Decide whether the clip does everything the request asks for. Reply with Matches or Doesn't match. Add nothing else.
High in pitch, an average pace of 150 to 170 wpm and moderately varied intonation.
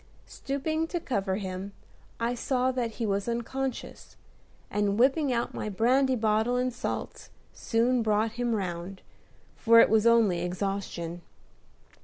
Doesn't match